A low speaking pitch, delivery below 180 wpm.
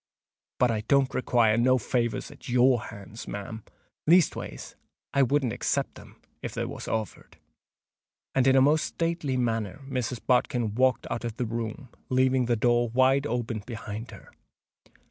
Yes: low, 125 Hz; average, 150 wpm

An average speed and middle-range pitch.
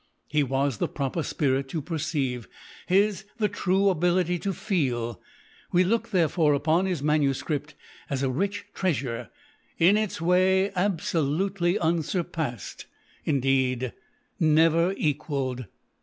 No: slow, 125 wpm; medium, 160 Hz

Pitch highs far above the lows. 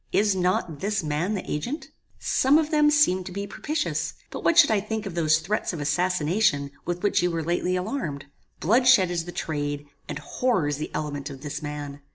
Yes: wide, 6.0 semitones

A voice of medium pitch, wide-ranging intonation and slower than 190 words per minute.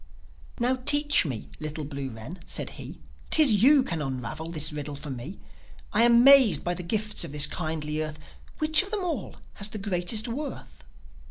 Yes: medium, 180 Hz; wide, 8.7 semitones; average, 180 wpm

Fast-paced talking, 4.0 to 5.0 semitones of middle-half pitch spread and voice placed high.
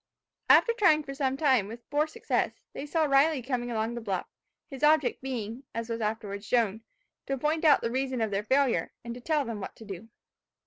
Yes: fast, 210 wpm; average, 4.4 semitones; very high, 250 Hz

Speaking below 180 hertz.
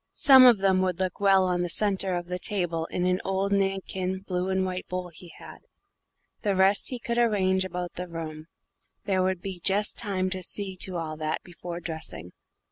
No: medium, 185 Hz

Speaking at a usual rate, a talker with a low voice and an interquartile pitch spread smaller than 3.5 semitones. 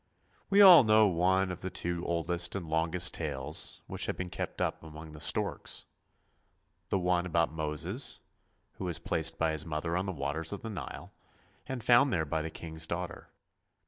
Yes: average, 180 wpm; very low, 85 Hz; average, 2.8 semitones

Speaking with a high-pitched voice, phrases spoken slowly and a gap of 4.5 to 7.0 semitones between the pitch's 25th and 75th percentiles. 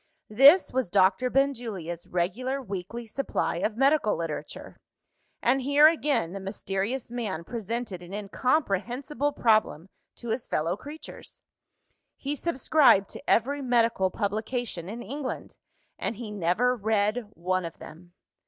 Yes: high, 225 Hz; slow, 125 wpm; average, 5.3 semitones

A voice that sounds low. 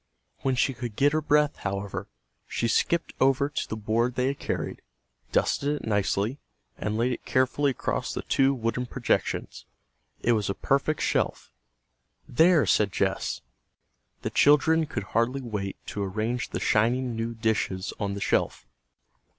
Yes: low, 120 Hz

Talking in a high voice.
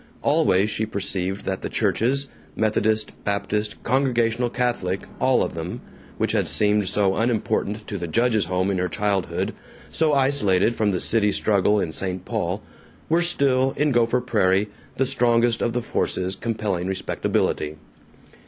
No: low, 105 Hz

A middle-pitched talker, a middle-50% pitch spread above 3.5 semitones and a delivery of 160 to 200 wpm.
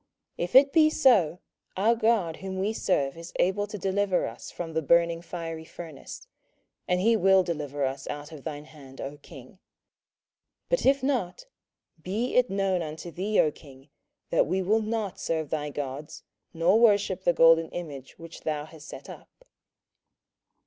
Yes: medium, 175 Hz; average, 4.8 semitones; average, 170 wpm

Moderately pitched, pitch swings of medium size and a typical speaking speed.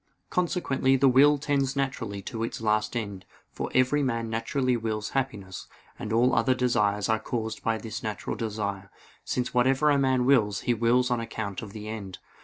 No: low, 115 Hz; average, 3.5 semitones; average, 180 wpm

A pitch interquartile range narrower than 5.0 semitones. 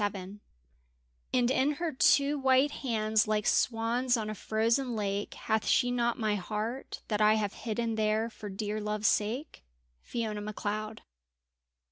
Yes: narrow, 2.6 semitones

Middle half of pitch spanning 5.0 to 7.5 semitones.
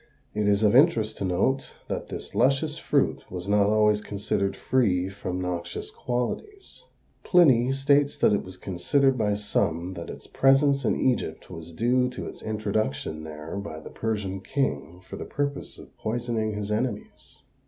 Yes: wide, 5.5 semitones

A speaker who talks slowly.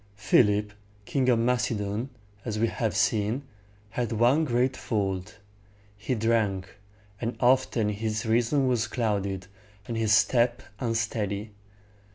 Yes: slow, 120 wpm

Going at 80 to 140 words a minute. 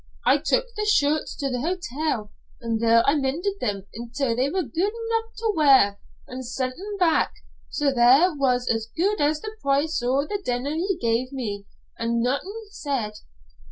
No: average, 175 wpm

